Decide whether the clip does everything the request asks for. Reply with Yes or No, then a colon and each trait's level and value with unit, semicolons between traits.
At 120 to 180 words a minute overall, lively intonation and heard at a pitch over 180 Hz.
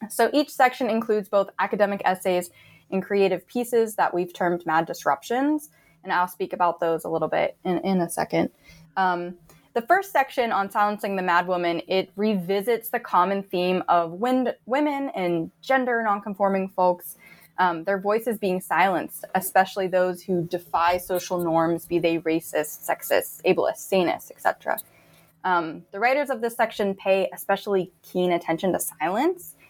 No: average, 160 wpm; average, 3.7 semitones; high, 190 Hz